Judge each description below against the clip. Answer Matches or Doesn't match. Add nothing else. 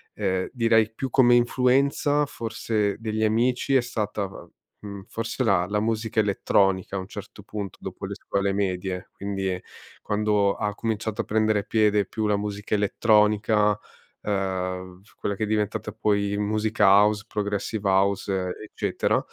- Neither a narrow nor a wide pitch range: Doesn't match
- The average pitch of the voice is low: Matches